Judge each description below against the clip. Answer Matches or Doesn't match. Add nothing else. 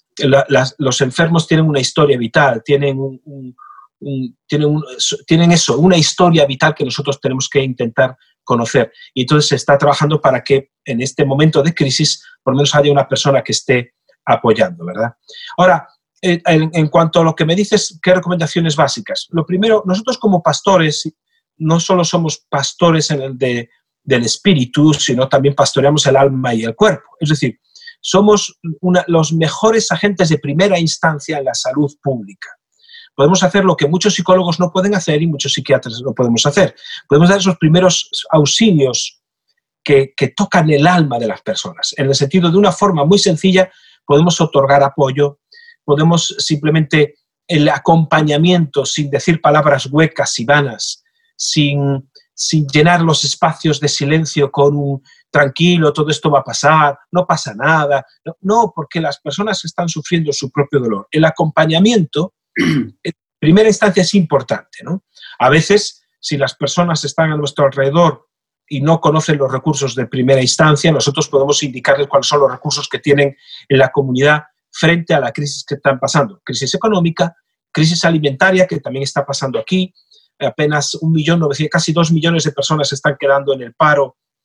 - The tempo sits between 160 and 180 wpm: Matches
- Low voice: Doesn't match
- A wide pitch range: Doesn't match